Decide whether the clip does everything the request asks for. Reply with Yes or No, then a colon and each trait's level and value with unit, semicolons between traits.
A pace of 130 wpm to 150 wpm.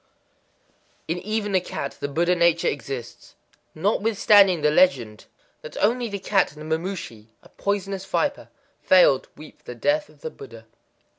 No: average, 165 wpm